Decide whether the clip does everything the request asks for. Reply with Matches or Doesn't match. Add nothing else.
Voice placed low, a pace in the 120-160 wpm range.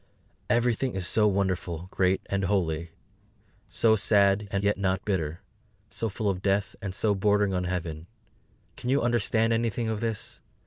Matches